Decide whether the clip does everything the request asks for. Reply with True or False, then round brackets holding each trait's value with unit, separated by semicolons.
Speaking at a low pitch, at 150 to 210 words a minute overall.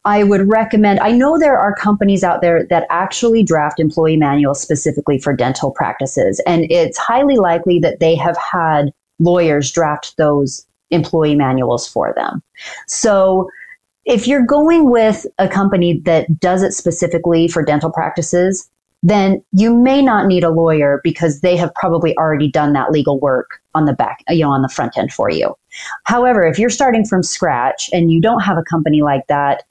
False (170 Hz; 180 wpm)